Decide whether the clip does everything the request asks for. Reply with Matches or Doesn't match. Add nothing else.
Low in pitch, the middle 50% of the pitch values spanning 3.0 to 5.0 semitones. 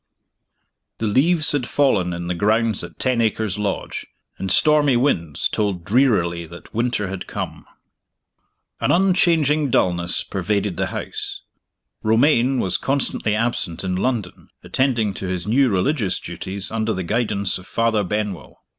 Doesn't match